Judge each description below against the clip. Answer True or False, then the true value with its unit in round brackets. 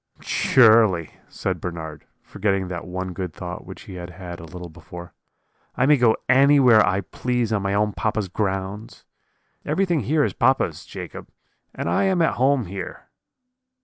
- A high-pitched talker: False (100 Hz)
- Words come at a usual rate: True (160 wpm)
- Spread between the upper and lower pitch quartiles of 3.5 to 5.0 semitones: False (5.6 semitones)